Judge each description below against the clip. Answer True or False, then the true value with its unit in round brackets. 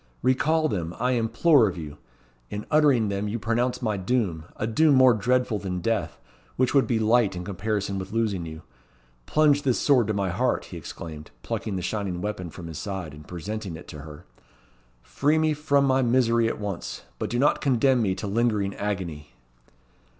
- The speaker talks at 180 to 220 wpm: True (185 wpm)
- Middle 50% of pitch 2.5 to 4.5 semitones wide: False (5.4 semitones)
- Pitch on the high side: False (110 Hz)